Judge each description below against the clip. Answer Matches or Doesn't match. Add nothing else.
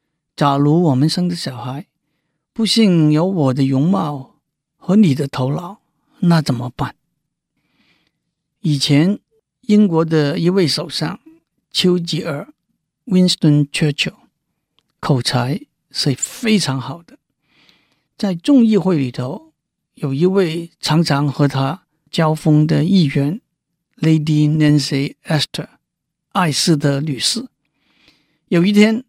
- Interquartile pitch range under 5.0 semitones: Matches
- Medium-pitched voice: Matches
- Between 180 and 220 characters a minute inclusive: Matches